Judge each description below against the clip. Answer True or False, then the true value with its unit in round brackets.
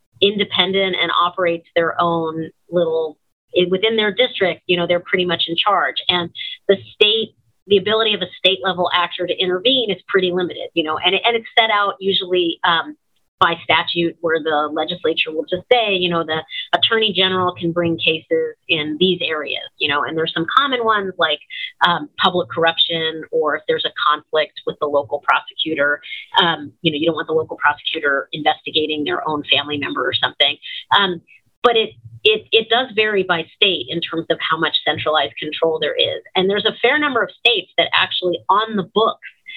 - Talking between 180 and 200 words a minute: True (190 wpm)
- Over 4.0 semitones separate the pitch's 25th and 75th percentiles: True (4.6 semitones)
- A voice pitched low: False (180 Hz)